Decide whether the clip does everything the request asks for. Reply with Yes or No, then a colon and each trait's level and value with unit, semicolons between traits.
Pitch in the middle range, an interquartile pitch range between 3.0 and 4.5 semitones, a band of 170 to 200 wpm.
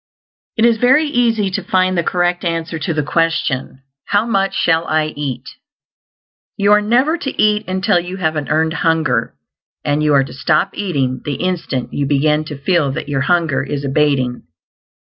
No: medium, 165 Hz; average, 5.1 semitones; average, 180 wpm